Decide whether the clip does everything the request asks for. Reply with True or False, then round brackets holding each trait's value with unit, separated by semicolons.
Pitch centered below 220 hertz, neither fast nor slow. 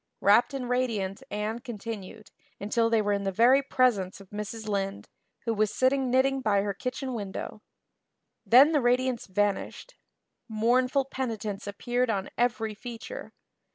False (225 Hz; 145 wpm)